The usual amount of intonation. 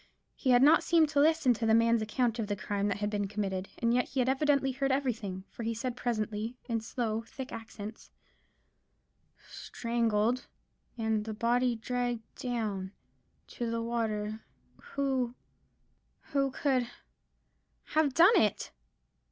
Yes: average, 3.0 semitones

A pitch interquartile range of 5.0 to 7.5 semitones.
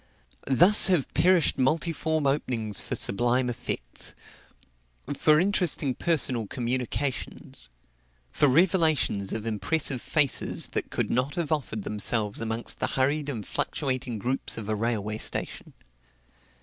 Yes: wide, 5.5 semitones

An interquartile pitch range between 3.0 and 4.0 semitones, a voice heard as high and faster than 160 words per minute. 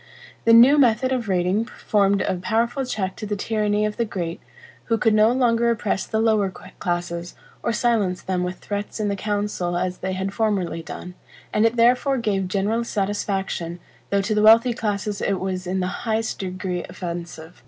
Yes: average, 3.4 semitones; high, 205 Hz; average, 185 wpm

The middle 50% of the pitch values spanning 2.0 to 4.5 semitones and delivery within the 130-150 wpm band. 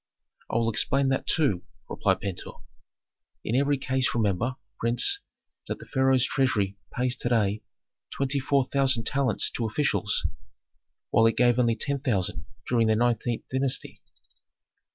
Yes: average, 3.0 semitones; average, 140 wpm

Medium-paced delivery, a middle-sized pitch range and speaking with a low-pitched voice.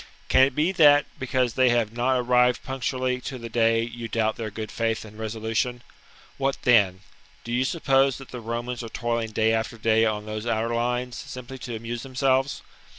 No: average, 195 wpm; narrow, 2.3 semitones; low, 120 Hz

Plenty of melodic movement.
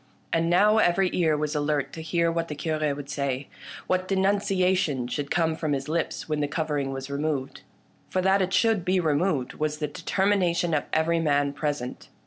No: average, 3.9 semitones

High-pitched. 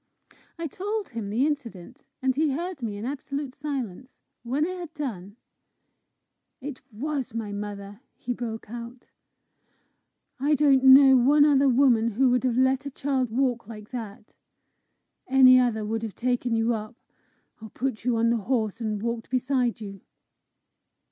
Yes: very high, 250 Hz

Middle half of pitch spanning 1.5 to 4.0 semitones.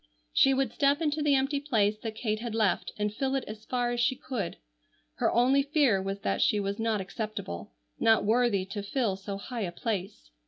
No: average, 4.7 semitones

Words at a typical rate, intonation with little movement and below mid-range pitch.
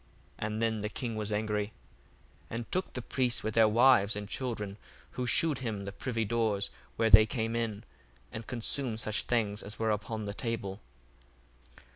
Yes: average, 175 wpm; narrow, 2.0 semitones; low, 110 Hz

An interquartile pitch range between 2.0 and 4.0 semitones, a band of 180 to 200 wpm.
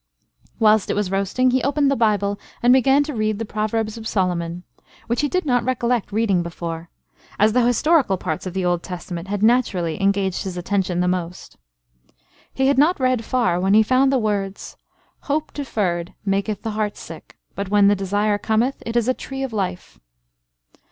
No: average, 4.7 semitones; average, 185 wpm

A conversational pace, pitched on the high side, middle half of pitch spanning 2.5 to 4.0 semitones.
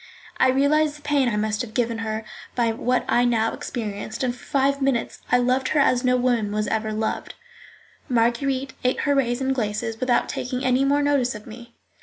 Yes: average, 195 wpm; high, 245 Hz; average, 2.9 semitones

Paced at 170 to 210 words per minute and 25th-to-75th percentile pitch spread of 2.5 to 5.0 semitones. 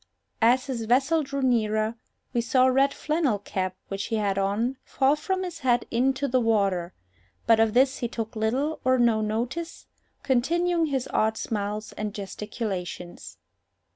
No: average, 160 wpm; average, 3.9 semitones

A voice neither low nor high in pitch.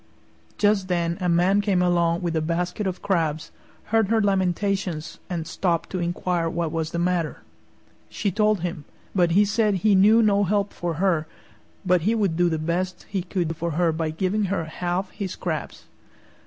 Yes: medium, 180 Hz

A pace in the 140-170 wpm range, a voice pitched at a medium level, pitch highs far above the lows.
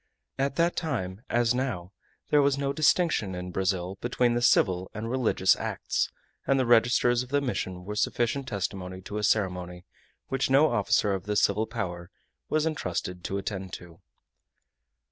No: average, 165 wpm; low, 105 Hz; wide, 5.9 semitones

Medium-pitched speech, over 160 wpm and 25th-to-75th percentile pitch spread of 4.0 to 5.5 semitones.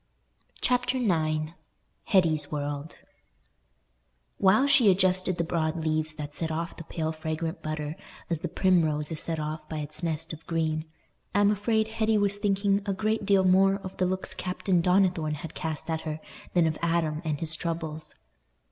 No: medium, 165 Hz; average, 170 wpm; average, 3.5 semitones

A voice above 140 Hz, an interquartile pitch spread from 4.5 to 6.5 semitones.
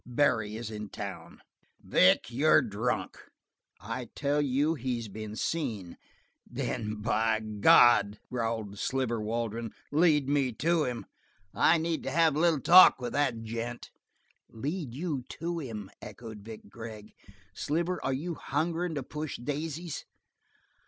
No: low, 125 Hz; wide, 5.4 semitones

